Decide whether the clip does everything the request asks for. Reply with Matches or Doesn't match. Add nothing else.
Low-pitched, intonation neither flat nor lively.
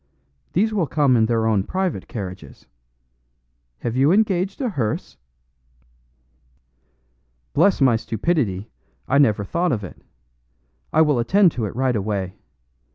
Doesn't match